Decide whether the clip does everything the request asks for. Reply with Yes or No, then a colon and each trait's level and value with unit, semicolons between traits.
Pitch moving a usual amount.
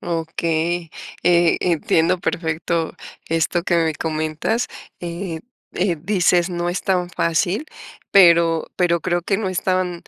No: narrow, 1.6 semitones